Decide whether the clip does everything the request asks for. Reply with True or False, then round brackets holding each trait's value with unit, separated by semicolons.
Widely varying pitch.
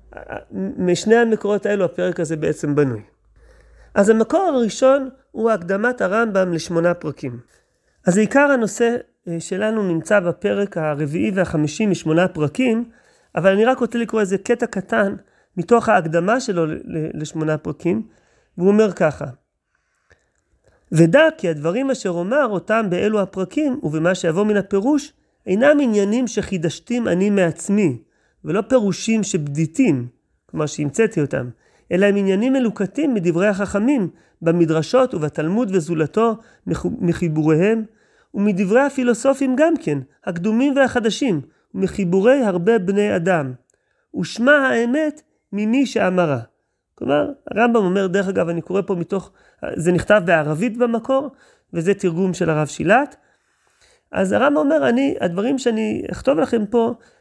True (5.7 semitones)